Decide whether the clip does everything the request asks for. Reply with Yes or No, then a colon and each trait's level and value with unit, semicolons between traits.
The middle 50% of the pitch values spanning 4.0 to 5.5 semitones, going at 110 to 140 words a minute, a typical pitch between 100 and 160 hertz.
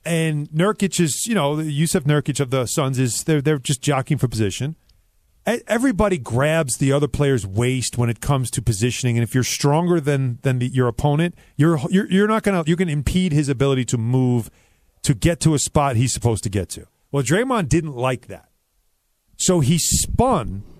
No: average, 5.1 semitones; average, 200 wpm; medium, 140 Hz